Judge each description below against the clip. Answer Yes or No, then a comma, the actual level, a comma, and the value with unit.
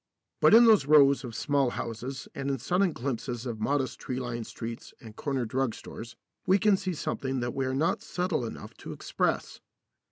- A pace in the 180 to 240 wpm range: Yes, average, 190 wpm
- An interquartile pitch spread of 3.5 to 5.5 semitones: Yes, average, 4.0 semitones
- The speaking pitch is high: No, low, 135 Hz